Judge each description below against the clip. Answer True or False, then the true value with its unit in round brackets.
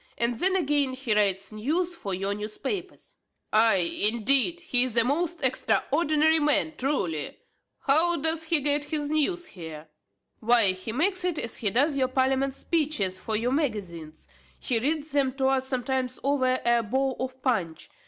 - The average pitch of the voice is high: True (260 Hz)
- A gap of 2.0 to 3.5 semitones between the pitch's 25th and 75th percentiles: False (5.3 semitones)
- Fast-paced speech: False (165 wpm)